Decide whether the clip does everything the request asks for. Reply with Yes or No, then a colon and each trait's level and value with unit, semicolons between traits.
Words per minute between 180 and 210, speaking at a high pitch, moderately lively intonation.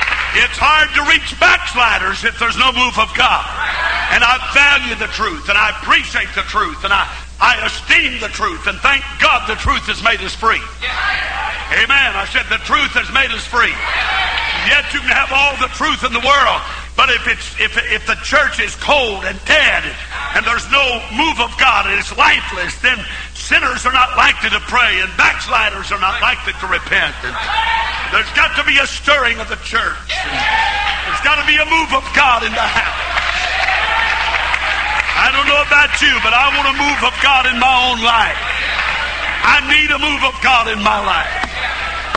Yes: average, 195 wpm; very high, 275 Hz; average, 3.4 semitones